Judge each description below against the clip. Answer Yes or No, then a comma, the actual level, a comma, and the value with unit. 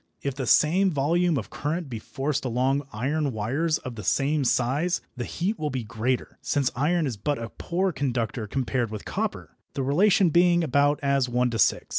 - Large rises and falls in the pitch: No, average, 4.2 semitones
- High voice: No, medium, 140 Hz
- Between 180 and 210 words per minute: Yes, average, 190 wpm